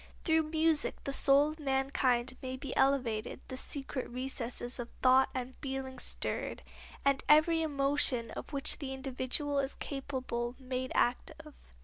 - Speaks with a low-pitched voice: No, very high, 270 Hz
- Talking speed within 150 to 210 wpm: No, average, 140 wpm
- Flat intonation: Yes, narrow, 2.0 semitones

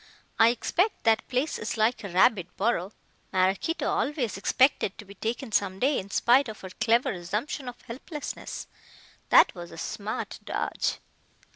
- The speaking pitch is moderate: No, high, 220 Hz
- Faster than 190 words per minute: No, average, 155 wpm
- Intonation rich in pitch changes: No, average, 4.6 semitones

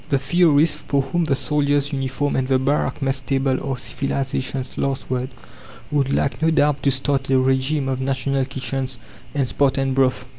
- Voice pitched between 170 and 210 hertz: No, low, 135 Hz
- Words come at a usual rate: Yes, average, 175 wpm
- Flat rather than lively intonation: Yes, narrow, 1.3 semitones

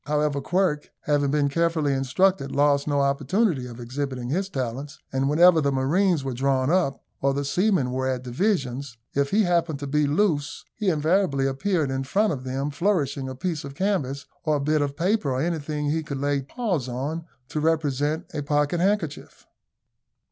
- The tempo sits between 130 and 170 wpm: No, average, 180 wpm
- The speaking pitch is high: No, medium, 145 Hz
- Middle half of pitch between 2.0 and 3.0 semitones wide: No, average, 3.6 semitones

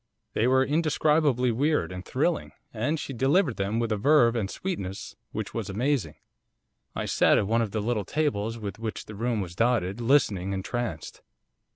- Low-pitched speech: Yes, low, 115 Hz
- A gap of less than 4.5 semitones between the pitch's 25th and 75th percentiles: No, average, 5.2 semitones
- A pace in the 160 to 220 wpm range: Yes, average, 175 wpm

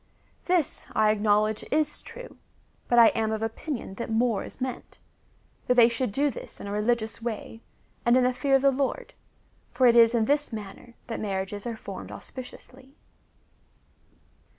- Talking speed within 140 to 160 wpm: No, average, 175 wpm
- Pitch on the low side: No, high, 235 Hz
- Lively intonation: No, average, 3.2 semitones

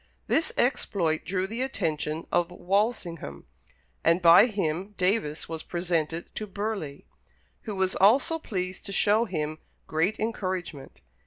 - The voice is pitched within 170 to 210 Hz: Yes, medium, 185 Hz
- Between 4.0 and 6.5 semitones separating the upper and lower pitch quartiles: Yes, average, 4.3 semitones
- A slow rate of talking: Yes, slow, 130 wpm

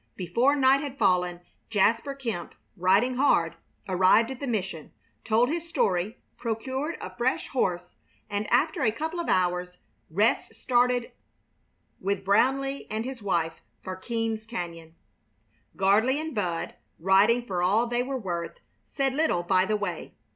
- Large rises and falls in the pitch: Yes, wide, 6.0 semitones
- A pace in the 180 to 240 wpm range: No, average, 145 wpm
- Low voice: No, high, 220 Hz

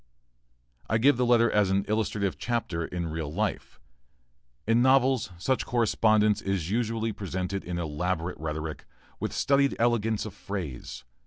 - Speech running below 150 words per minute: Yes, average, 140 wpm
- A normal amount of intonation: Yes, average, 4.8 semitones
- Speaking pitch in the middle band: No, low, 105 Hz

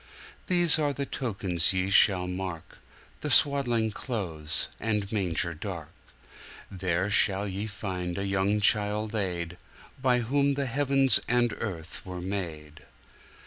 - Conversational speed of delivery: No, slow, 115 wpm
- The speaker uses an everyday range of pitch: Yes, average, 4.8 semitones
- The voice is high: No, low, 100 Hz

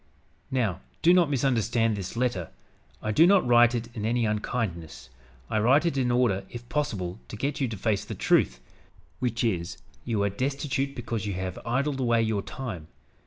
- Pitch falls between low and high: No, low, 115 Hz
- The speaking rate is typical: Yes, average, 185 wpm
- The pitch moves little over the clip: No, average, 4.4 semitones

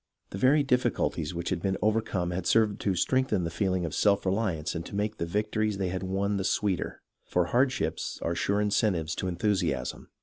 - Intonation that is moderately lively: Yes, average, 3.4 semitones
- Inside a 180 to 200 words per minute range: Yes, average, 195 wpm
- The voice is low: Yes, very low, 95 Hz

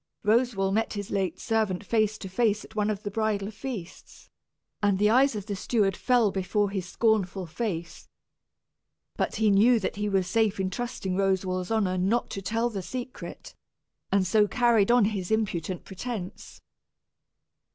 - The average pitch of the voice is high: Yes, high, 205 Hz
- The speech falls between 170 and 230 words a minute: No, average, 160 wpm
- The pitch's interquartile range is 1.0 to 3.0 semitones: Yes, average, 2.7 semitones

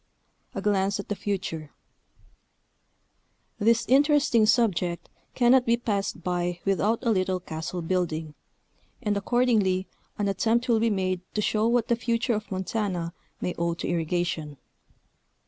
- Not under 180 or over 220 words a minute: No, slow, 135 wpm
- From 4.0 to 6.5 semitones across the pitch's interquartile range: Yes, average, 4.5 semitones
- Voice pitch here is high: Yes, high, 200 Hz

